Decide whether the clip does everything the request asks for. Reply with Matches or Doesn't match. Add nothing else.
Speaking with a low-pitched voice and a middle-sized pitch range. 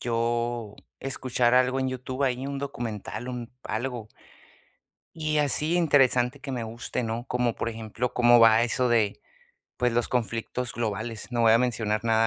Doesn't match